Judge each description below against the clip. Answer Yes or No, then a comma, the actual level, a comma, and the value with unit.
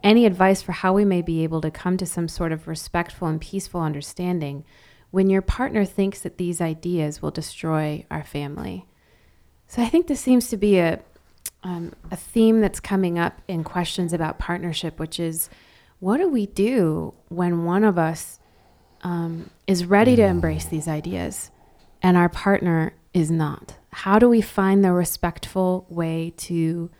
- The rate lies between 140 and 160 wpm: No, average, 170 wpm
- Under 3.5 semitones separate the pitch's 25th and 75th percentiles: Yes, average, 3.1 semitones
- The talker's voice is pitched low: No, medium, 175 Hz